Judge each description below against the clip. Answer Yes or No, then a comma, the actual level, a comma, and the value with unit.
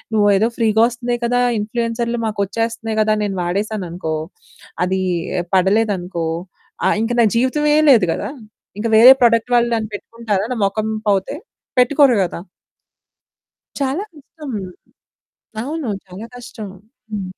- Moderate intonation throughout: Yes, average, 3.3 semitones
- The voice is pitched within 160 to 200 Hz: No, high, 225 Hz